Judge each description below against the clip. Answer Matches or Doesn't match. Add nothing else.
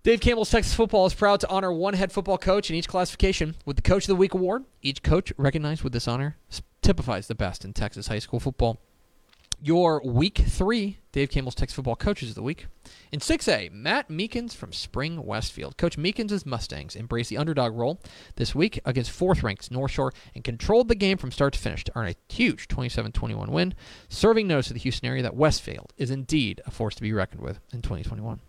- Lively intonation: Matches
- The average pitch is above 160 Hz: Doesn't match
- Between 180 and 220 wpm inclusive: Matches